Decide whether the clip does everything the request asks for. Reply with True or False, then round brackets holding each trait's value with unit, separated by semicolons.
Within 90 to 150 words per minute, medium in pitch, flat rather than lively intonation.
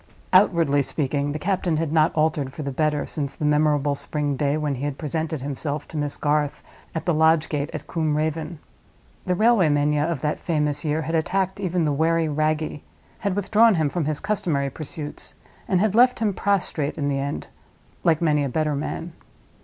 False (195 wpm; 155 Hz; 2.3 semitones)